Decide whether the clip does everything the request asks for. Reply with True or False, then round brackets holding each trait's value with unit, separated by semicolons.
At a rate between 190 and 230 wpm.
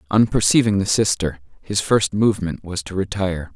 False (170 wpm)